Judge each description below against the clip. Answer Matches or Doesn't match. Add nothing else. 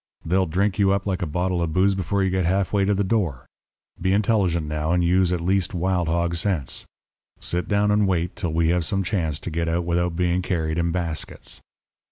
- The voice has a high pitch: Doesn't match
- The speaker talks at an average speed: Doesn't match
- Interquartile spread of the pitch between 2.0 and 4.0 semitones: Matches